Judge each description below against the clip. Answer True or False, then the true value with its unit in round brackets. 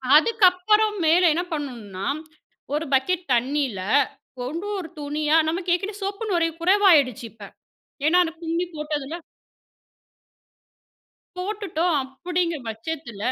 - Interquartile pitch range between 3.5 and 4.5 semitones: True (4.2 semitones)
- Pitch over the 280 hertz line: True (325 Hz)